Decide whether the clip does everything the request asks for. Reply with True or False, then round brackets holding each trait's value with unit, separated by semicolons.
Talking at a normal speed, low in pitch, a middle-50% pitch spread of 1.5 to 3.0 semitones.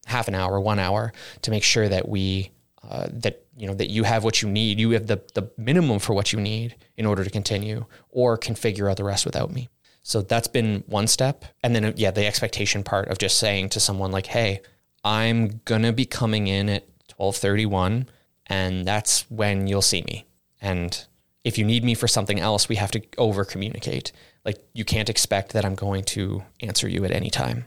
False (210 wpm; 105 Hz; 2.5 semitones)